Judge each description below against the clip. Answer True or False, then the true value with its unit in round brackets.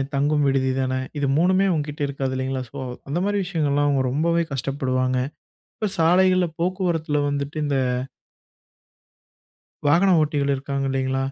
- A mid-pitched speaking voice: True (145 Hz)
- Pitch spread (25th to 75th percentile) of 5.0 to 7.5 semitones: False (3.9 semitones)